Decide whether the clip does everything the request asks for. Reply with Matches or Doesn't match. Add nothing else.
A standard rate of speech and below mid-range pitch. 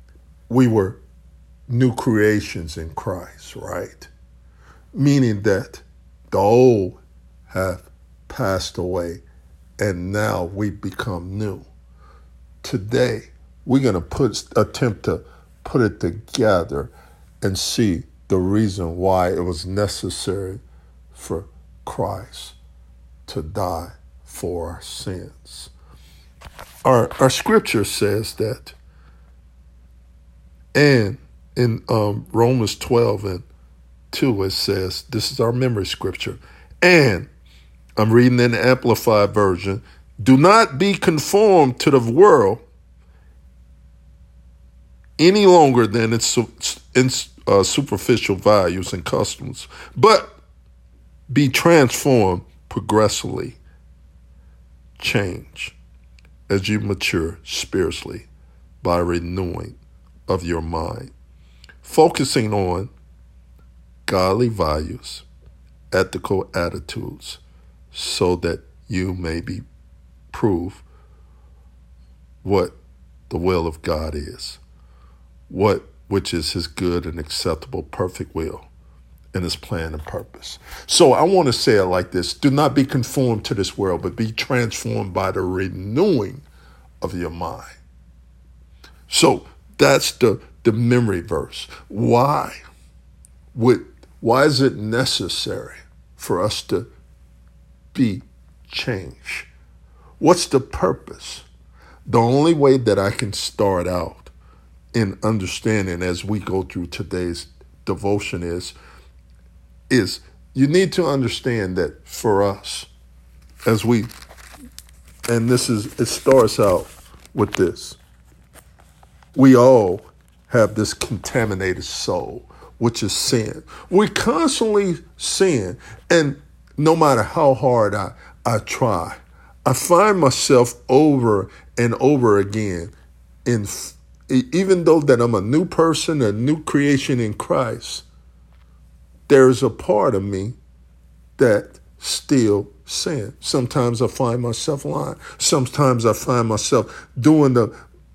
Doesn't match